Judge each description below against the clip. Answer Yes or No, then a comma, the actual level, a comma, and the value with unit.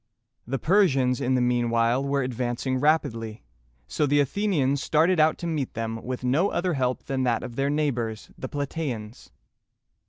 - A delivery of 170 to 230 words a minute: Yes, average, 175 wpm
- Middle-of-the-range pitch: No, low, 130 Hz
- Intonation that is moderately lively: Yes, average, 3.6 semitones